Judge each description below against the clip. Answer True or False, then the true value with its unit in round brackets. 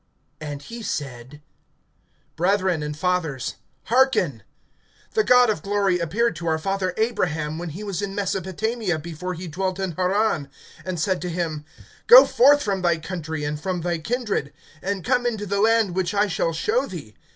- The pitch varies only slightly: False (4.4 semitones)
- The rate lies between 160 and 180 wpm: True (170 wpm)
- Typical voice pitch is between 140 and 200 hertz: True (185 Hz)